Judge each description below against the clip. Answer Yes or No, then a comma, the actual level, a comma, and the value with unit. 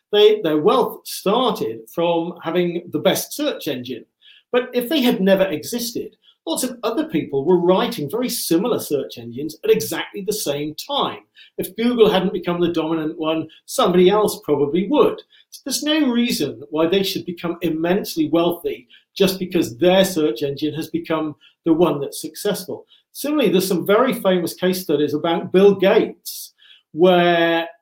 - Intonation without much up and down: No, average, 5.2 semitones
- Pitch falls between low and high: Yes, medium, 180 Hz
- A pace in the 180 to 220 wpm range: No, average, 160 wpm